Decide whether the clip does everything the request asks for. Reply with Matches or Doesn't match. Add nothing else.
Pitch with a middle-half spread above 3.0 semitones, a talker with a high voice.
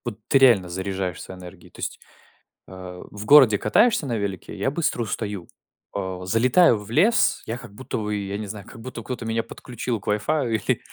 Doesn't match